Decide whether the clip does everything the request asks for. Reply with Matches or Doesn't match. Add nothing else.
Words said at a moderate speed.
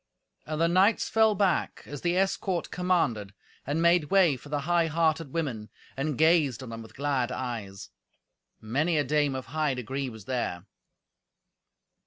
Matches